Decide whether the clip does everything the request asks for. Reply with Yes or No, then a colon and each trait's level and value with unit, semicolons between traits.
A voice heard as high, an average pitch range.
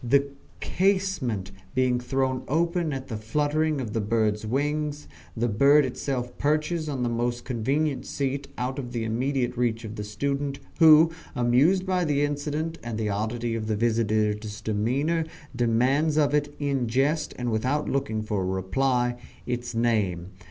No: low, 125 Hz; average, 4.4 semitones